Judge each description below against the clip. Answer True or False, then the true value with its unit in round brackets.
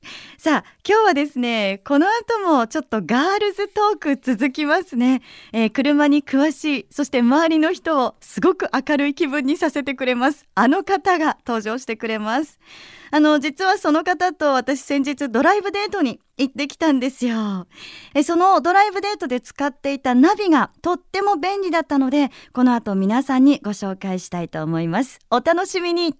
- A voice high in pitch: True (290 Hz)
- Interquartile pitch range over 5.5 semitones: False (5.1 semitones)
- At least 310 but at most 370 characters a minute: True (340 characters per minute)